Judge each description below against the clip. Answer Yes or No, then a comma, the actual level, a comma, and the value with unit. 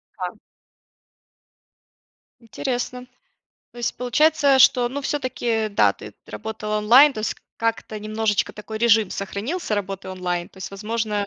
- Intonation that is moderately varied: Yes, average, 3.1 semitones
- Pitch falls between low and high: No, high, 220 Hz